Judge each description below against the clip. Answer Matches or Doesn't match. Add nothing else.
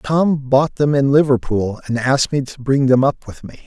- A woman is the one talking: Doesn't match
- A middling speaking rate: Doesn't match